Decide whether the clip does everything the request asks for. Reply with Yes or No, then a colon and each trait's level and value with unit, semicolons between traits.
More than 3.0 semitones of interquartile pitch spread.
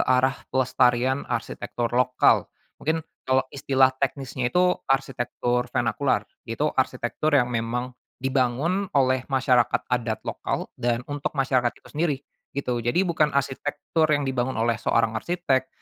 No: narrow, 2.4 semitones